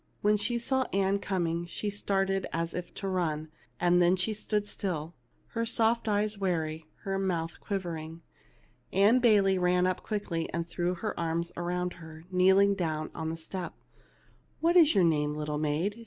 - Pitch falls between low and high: Yes, medium, 180 Hz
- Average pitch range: Yes, average, 3.5 semitones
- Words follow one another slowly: No, average, 170 wpm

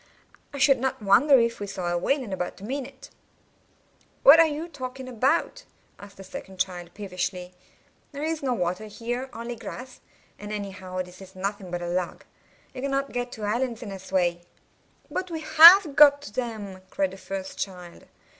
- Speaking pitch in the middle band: No, high, 215 Hz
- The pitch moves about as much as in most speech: No, wide, 6.3 semitones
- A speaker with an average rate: Yes, average, 185 wpm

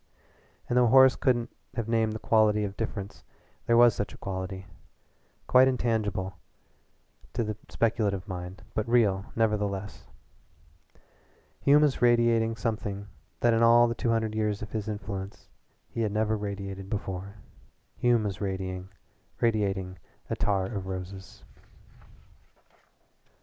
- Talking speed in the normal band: No, slow, 125 wpm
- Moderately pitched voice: No, low, 105 Hz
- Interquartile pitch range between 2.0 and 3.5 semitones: Yes, average, 3.0 semitones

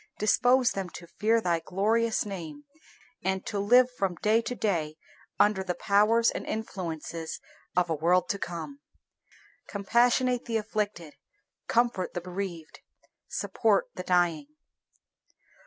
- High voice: Yes, high, 200 Hz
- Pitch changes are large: No, average, 4.6 semitones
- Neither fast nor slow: No, slow, 125 wpm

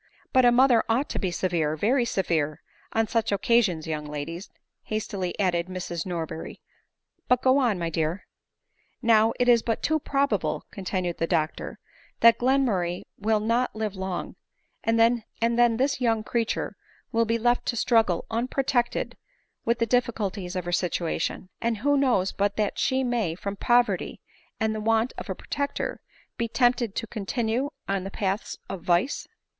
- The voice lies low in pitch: No, high, 220 Hz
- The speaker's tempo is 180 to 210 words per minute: No, average, 170 wpm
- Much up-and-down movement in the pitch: No, average, 4.6 semitones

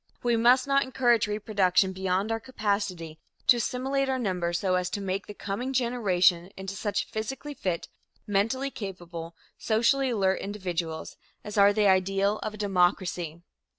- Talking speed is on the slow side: No, average, 150 wpm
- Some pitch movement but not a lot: Yes, average, 4.3 semitones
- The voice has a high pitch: Yes, high, 200 Hz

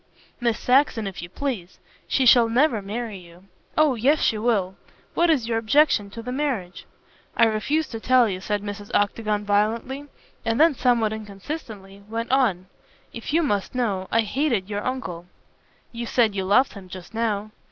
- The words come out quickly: No, average, 175 wpm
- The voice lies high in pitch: Yes, high, 225 Hz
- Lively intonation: No, average, 4.0 semitones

